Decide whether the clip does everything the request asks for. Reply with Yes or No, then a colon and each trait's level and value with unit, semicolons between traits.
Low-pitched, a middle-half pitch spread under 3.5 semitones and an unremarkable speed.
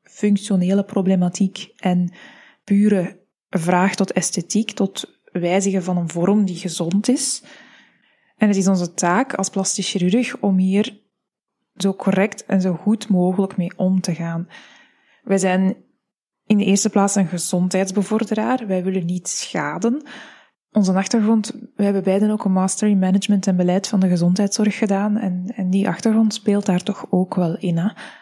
No: high, 195 Hz; narrow, 2.4 semitones; average, 155 wpm